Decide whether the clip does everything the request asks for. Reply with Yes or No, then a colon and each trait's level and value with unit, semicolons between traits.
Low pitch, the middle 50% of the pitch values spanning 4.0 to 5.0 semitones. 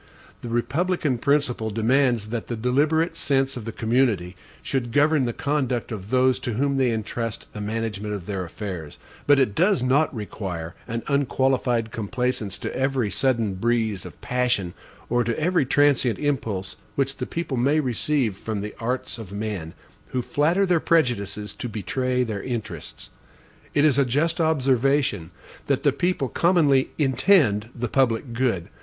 Yes: low, 125 Hz; average, 4.3 semitones